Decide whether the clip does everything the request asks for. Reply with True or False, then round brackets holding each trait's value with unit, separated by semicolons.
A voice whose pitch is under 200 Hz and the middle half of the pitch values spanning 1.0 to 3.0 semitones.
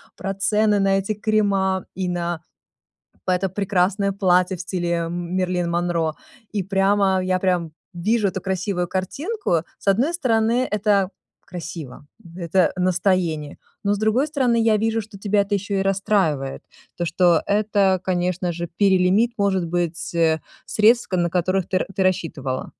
True (190 Hz; 2.6 semitones)